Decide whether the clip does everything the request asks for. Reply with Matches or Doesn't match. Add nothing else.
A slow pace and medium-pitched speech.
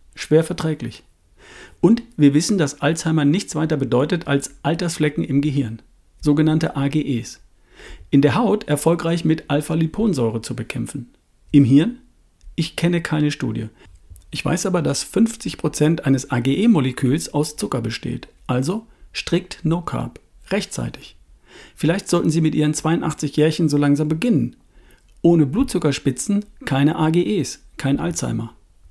Matches